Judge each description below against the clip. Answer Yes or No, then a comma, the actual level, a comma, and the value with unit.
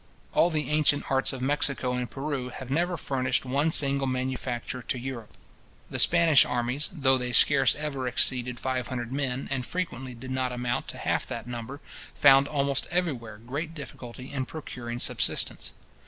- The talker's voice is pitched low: Yes, low, 130 Hz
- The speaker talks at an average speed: Yes, average, 165 wpm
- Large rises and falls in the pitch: No, narrow, 2.4 semitones